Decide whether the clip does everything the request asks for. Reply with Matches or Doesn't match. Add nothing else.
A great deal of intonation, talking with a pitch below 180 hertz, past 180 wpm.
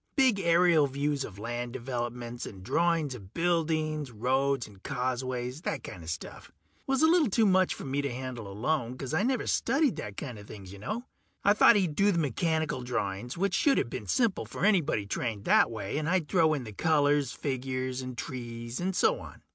Matches